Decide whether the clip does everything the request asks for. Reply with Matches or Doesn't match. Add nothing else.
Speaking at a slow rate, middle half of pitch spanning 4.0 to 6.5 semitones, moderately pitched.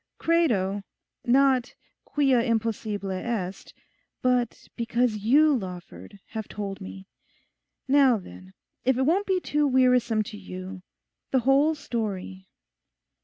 Doesn't match